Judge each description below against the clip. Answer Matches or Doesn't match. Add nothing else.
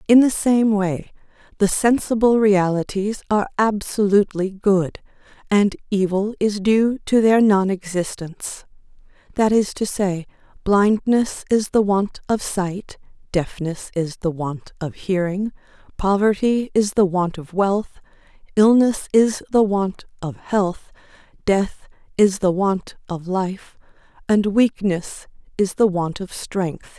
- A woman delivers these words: Matches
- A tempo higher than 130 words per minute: Doesn't match